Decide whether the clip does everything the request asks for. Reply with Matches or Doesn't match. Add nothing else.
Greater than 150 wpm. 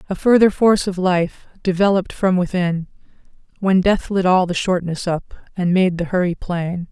Matches